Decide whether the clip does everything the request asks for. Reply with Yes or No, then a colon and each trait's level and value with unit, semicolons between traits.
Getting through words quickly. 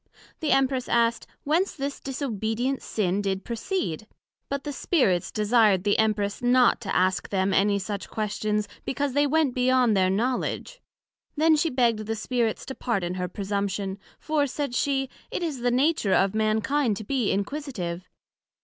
No: average, 160 wpm